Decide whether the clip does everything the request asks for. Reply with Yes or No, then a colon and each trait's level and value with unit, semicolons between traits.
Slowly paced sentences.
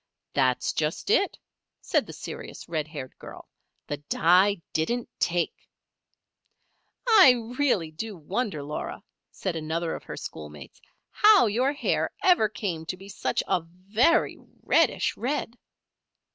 Yes: slow, 130 wpm